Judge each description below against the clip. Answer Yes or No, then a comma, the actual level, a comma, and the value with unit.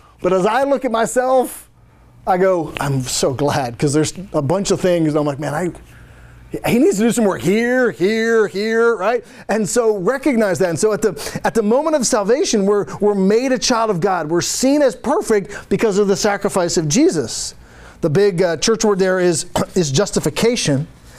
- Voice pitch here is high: Yes, high, 205 Hz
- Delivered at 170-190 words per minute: No, average, 200 wpm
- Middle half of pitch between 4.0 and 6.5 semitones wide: Yes, average, 4.4 semitones